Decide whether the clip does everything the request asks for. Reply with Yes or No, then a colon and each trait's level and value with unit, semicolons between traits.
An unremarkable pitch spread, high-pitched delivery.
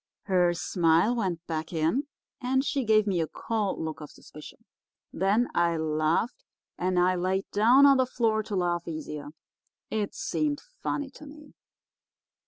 No: wide, 6.8 semitones; high, 195 Hz